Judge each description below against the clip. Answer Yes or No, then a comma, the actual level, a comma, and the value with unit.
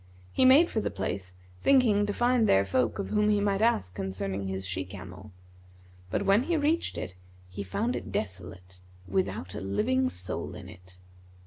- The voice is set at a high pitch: No, low, 100 Hz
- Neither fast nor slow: Yes, average, 180 wpm